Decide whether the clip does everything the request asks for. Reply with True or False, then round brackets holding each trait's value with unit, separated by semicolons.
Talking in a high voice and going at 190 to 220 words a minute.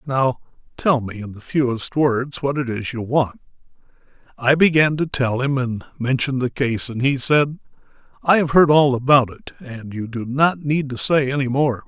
False (135 Hz; 195 wpm)